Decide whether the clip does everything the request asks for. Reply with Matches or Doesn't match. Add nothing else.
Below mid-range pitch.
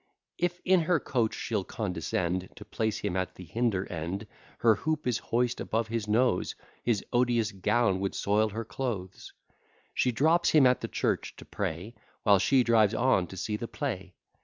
Matches